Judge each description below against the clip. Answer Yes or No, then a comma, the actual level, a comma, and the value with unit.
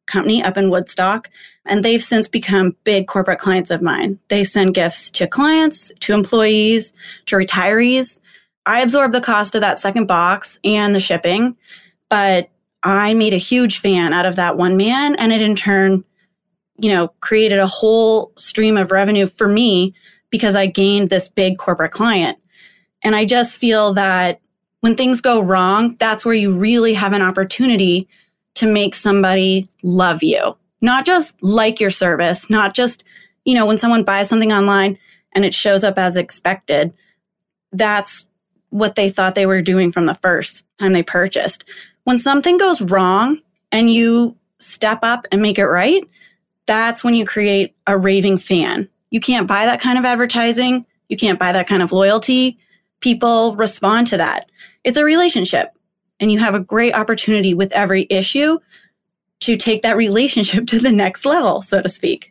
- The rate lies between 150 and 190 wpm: Yes, average, 170 wpm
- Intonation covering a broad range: No, average, 3.2 semitones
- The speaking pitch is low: No, high, 205 Hz